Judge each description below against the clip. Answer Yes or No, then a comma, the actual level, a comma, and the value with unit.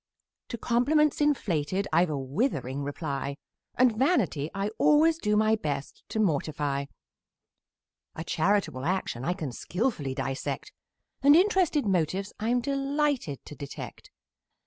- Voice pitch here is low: No, high, 195 Hz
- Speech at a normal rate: No, slow, 125 wpm